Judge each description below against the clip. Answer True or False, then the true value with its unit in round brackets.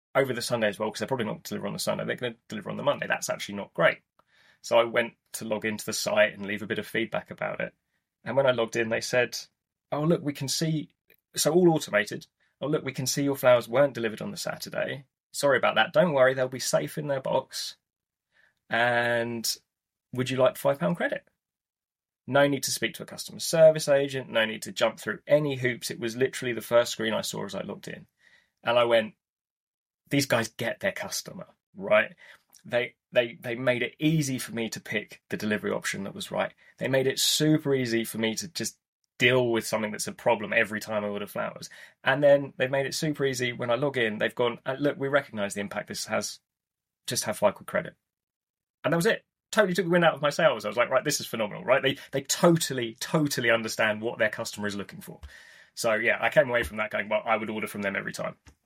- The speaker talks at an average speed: False (235 wpm)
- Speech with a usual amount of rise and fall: True (3.7 semitones)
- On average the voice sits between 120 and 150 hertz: True (125 Hz)